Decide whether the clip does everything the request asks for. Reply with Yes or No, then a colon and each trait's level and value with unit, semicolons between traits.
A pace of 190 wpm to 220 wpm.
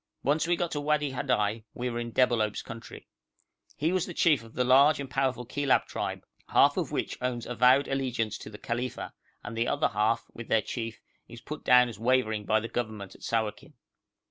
Yes: average, 195 wpm